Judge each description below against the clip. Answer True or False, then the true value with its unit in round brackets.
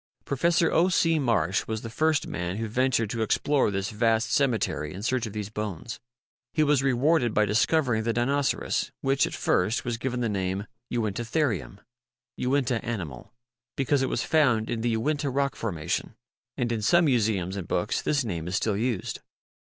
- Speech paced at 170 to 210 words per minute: True (175 wpm)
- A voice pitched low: True (115 Hz)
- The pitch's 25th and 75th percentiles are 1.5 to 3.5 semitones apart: False (4.6 semitones)